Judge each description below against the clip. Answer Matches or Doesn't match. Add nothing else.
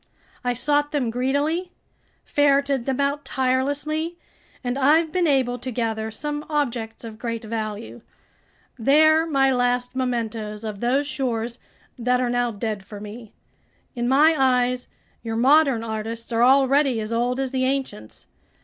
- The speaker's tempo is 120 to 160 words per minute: Matches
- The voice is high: Matches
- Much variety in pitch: Doesn't match